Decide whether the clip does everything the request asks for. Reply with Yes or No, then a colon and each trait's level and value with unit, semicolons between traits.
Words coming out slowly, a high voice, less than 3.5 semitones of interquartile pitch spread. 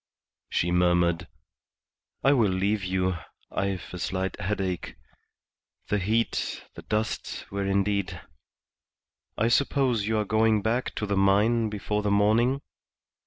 No: slow, 125 wpm; low, 100 Hz; average, 2.9 semitones